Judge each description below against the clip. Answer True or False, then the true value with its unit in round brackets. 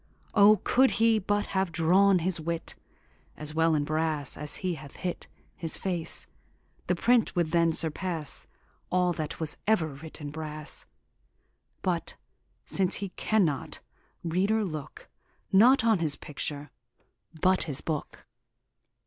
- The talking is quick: False (135 wpm)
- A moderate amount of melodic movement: True (3.7 semitones)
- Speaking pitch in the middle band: True (170 Hz)